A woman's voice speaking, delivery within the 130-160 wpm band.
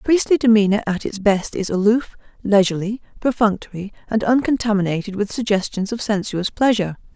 Yes: female; slow, 135 wpm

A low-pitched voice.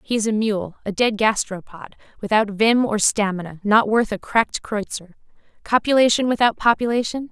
No: high, 215 Hz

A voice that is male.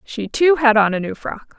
No: female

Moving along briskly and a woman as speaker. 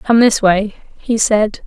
No: average, 180 wpm; female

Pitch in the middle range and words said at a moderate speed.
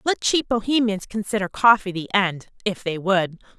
No: high, 205 Hz; average, 165 wpm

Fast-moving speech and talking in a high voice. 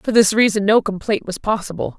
Yes: fast, 210 wpm; high, 205 Hz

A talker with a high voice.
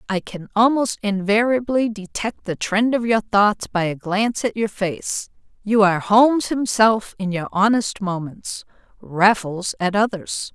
Yes: high, 210 Hz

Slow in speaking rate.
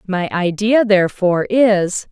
Yes: slow, 115 wpm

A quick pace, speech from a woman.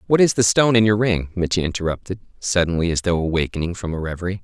No: fast, 215 wpm; male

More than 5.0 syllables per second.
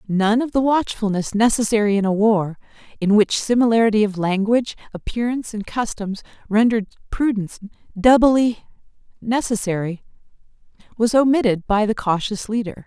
Yes: 5.5 syllables/s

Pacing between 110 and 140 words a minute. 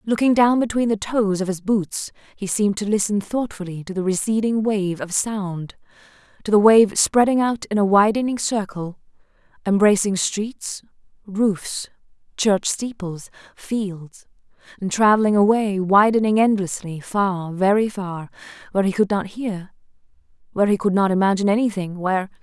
Yes: slow, 135 wpm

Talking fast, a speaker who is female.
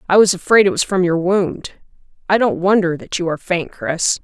Yes: fast, 225 wpm; female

